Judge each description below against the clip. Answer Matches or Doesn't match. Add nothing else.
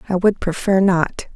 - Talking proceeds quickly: Doesn't match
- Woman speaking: Matches